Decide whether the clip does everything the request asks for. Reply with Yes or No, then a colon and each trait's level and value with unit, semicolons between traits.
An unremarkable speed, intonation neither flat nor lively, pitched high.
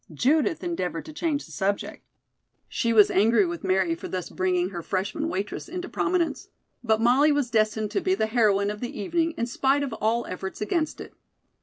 No: average, 190 wpm; wide, 7.1 semitones; high, 225 Hz